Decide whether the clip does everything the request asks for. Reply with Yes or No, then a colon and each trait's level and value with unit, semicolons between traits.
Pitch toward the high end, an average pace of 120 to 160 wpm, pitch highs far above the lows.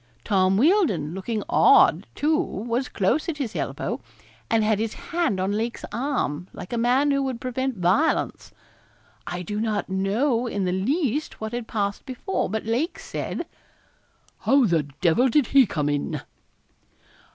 Yes: high, 225 Hz; average, 155 wpm; wide, 6.0 semitones